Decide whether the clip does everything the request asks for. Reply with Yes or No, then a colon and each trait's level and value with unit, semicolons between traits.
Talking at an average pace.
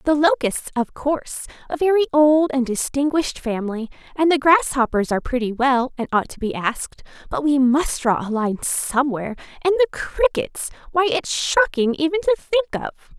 Yes: average, 165 wpm